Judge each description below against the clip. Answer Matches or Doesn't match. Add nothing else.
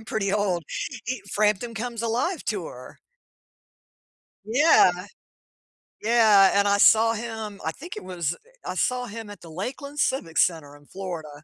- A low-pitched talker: Doesn't match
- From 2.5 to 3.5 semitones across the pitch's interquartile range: Doesn't match